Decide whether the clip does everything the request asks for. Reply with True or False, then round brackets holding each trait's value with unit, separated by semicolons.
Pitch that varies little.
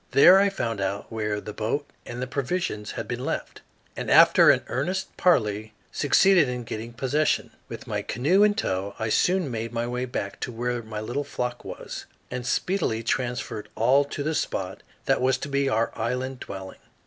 False (4.4 semitones)